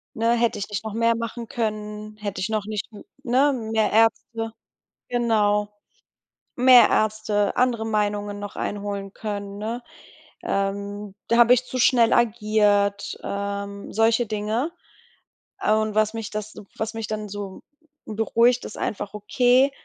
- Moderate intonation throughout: No, narrow, 2.0 semitones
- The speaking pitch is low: No, high, 215 Hz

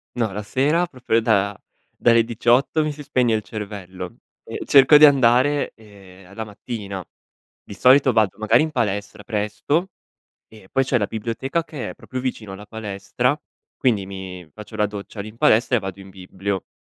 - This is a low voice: Yes, low, 110 Hz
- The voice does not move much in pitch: No, average, 4.3 semitones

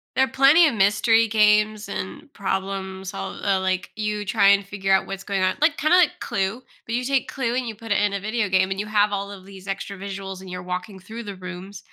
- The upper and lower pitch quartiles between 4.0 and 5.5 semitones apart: No, narrow, 2.6 semitones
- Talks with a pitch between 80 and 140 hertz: No, high, 200 Hz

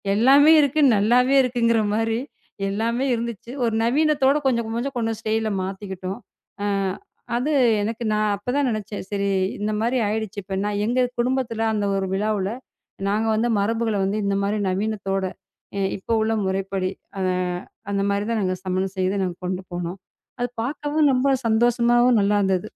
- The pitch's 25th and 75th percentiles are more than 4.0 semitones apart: No, average, 3.3 semitones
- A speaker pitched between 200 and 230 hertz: Yes, high, 220 Hz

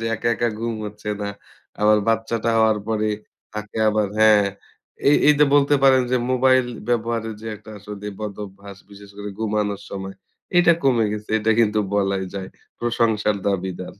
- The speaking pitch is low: Yes, low, 105 Hz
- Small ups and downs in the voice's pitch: Yes, narrow, 2.2 semitones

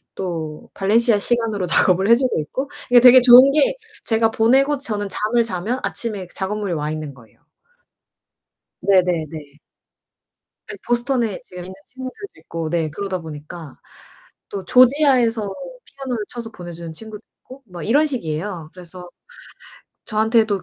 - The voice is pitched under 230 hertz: Yes, high, 210 Hz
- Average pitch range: No, wide, 5.7 semitones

